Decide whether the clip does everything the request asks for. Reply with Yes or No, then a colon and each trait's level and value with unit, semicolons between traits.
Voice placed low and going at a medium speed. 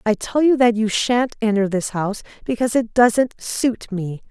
No: high, 225 Hz; average, 195 wpm